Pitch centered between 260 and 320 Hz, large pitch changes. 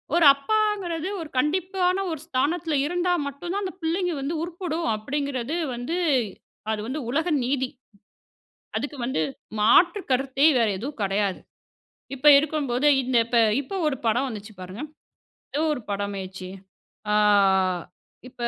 Yes: very high, 280 Hz; wide, 6.1 semitones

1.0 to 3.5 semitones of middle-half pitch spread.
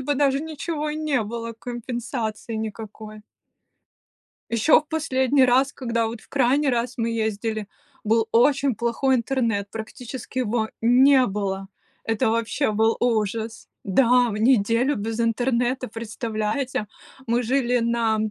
Yes: average, 3.0 semitones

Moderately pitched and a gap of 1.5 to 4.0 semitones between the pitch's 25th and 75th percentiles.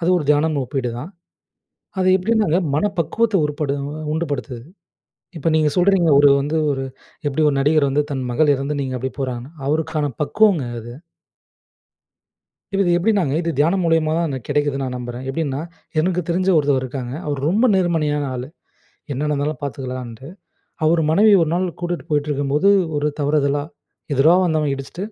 Yes: medium, 150 Hz; average, 3.6 semitones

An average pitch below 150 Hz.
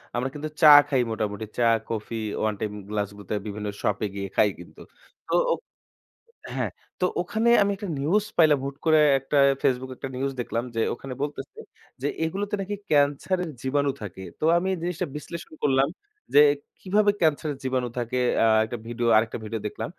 Yes: low, 135 Hz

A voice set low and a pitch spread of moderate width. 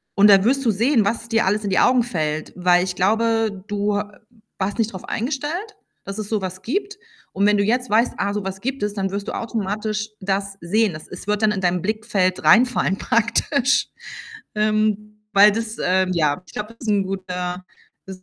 No: high, 210 Hz; average, 3.0 semitones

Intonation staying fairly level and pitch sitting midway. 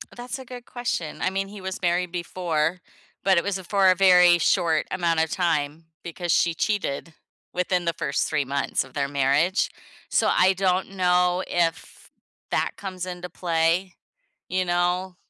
Yes: narrow, 2.2 semitones; medium, 180 Hz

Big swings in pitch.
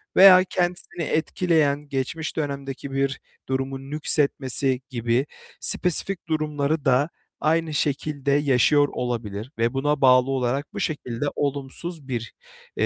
No: average, 2.7 semitones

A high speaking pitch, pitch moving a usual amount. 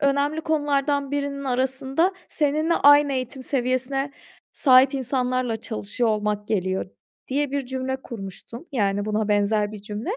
Yes: very high, 260 Hz; average, 4.5 semitones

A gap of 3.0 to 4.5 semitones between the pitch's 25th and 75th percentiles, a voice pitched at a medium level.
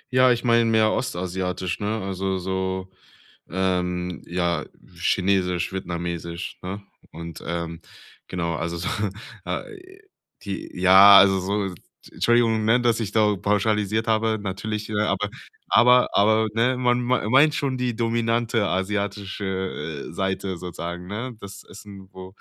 No: average, 3.5 semitones; low, 100 Hz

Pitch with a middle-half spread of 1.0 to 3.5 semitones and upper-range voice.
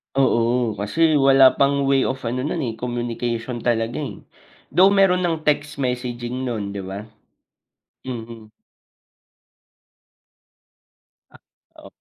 No: average, 3.2 semitones; low, 125 Hz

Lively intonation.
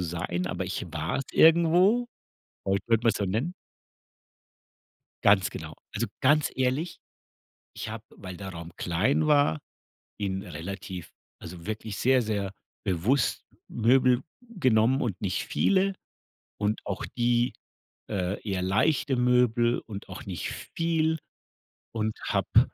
Yes: wide, 5.9 semitones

